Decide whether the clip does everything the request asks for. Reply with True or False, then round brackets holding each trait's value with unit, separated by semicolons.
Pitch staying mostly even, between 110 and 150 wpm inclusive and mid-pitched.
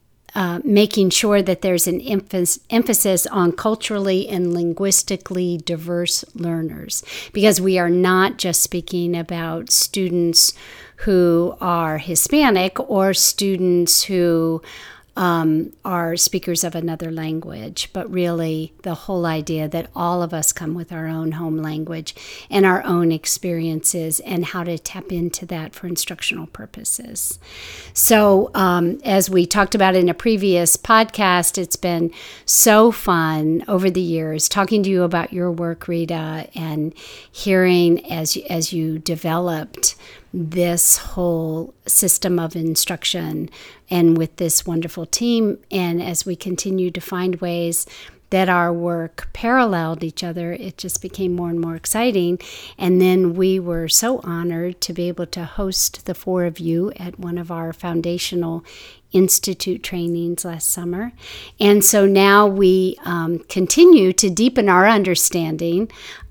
True (2.1 semitones; 140 wpm; 175 Hz)